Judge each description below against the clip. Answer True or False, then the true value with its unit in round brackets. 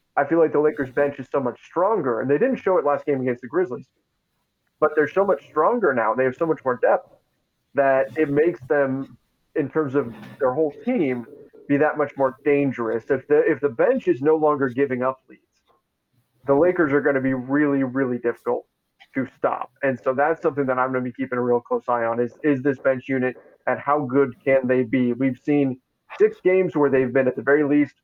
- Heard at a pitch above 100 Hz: True (140 Hz)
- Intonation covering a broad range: False (2.8 semitones)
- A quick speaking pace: True (225 wpm)